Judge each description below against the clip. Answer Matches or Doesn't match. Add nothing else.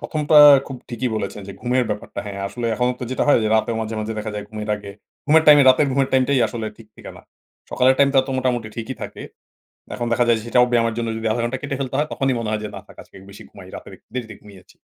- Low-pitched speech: Matches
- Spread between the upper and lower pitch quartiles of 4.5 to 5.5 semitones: Doesn't match